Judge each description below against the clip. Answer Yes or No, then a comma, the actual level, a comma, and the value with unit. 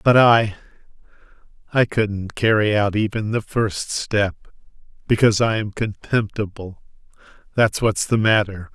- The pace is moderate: No, slow, 125 wpm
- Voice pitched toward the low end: Yes, low, 105 Hz